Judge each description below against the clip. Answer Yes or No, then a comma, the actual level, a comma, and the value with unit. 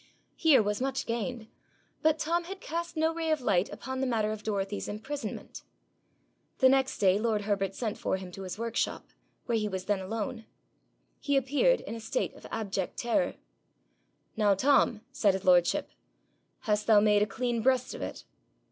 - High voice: Yes, high, 225 Hz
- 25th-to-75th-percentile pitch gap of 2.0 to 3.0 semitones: No, average, 4.6 semitones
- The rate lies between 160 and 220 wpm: Yes, average, 175 wpm